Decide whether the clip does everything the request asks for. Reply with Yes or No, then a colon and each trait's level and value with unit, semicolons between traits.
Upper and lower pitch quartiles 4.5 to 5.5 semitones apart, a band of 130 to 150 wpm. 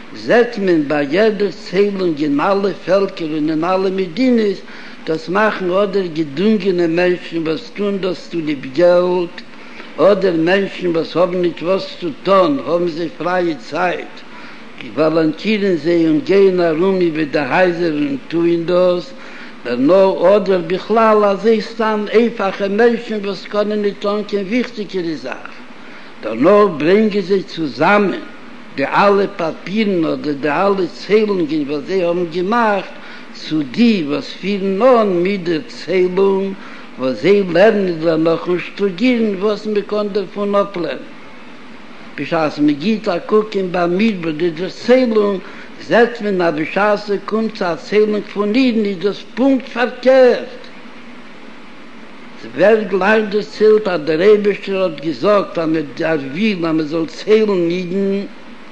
No: average, 3.9 semitones; average, 145 wpm